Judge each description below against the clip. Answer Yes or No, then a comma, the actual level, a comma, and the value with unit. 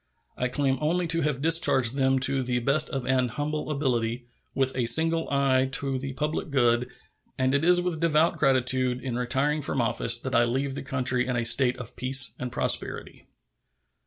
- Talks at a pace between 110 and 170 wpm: No, average, 190 wpm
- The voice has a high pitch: No, low, 130 Hz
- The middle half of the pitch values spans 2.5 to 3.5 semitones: Yes, average, 2.8 semitones